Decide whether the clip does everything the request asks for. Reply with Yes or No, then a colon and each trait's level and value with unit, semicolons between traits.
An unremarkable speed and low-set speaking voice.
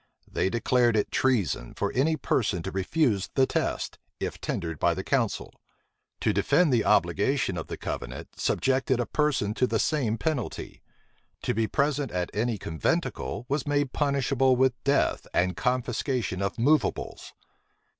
Yes: average, 150 wpm; low, 125 Hz